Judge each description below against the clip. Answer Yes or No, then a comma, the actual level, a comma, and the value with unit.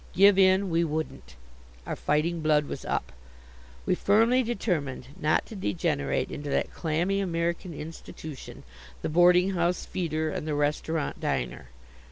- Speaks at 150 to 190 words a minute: No, average, 140 wpm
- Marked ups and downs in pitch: No, average, 3.7 semitones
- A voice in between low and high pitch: Yes, medium, 165 Hz